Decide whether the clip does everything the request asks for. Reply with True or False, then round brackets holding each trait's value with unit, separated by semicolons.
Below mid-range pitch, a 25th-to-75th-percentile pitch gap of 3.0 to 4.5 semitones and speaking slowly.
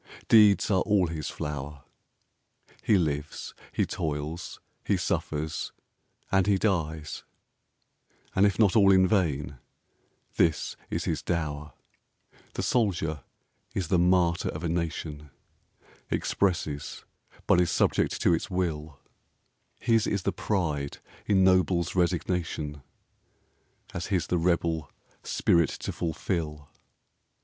True (85 Hz; 3.6 semitones; 115 wpm)